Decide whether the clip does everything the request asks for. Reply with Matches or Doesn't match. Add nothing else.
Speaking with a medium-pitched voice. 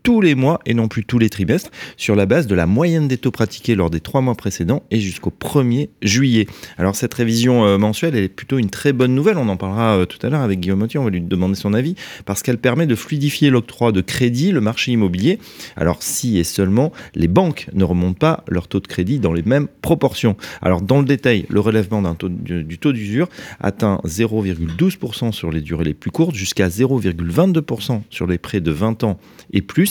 Doesn't match